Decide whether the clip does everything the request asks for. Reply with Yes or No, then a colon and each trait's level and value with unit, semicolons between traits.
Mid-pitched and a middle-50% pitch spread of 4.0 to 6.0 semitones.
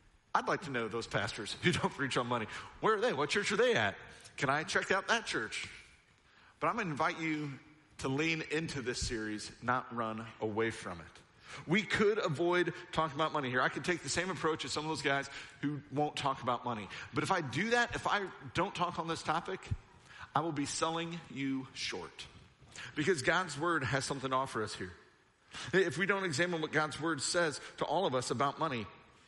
Yes: medium, 150 Hz; average, 4.6 semitones